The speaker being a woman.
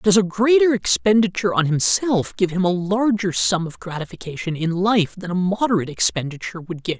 No: male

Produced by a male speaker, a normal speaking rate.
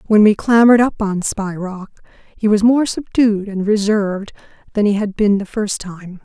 No: female; average, 190 wpm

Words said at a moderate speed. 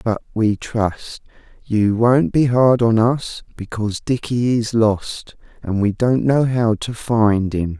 Yes: average, 160 wpm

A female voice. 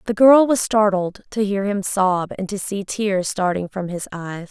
Yes: female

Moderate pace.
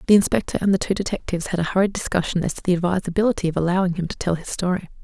No: fast, 250 wpm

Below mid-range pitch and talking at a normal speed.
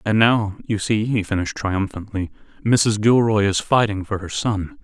Yes: low, 110 Hz; average, 175 wpm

